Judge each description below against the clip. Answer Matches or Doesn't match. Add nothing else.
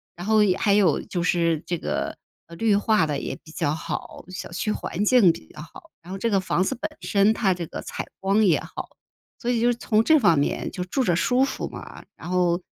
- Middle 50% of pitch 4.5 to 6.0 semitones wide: Doesn't match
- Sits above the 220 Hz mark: Doesn't match